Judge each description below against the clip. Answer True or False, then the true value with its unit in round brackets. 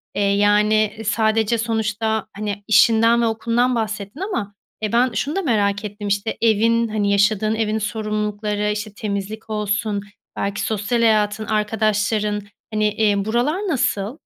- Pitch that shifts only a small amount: True (1.4 semitones)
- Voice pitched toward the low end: False (215 Hz)